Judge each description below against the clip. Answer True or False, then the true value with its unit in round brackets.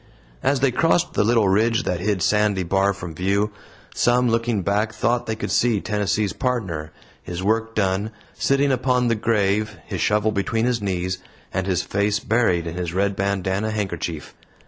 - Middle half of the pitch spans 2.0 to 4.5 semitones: True (3.2 semitones)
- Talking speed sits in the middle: True (170 wpm)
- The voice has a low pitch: True (105 Hz)